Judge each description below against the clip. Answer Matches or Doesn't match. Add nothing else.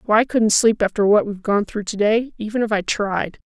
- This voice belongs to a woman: Matches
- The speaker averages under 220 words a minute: Doesn't match